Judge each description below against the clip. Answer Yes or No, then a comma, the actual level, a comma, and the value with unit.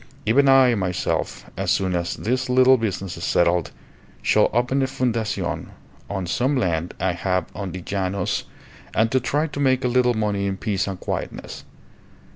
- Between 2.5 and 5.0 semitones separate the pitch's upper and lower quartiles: No, wide, 5.6 semitones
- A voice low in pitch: Yes, low, 105 Hz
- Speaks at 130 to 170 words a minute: Yes, average, 165 wpm